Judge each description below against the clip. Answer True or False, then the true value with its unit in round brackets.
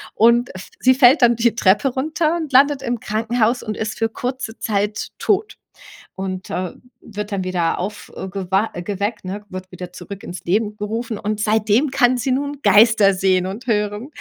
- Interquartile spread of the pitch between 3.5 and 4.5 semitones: True (3.9 semitones)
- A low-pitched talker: False (215 Hz)